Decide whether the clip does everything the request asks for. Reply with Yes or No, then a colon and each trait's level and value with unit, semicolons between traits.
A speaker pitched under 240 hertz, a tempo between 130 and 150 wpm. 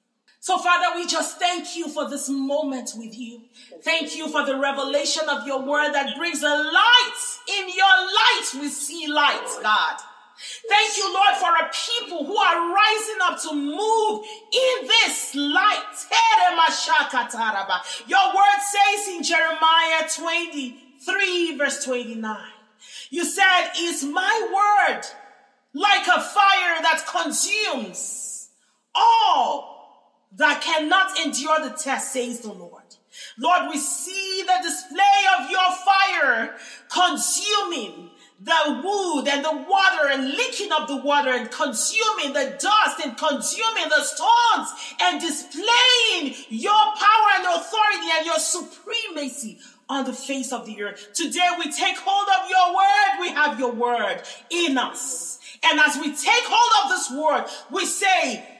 No: very high, 335 Hz; average, 140 wpm